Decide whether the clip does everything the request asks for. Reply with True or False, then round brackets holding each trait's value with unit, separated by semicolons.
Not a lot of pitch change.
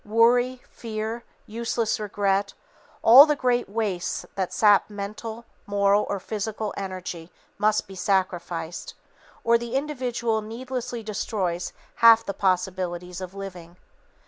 False (3.5 semitones)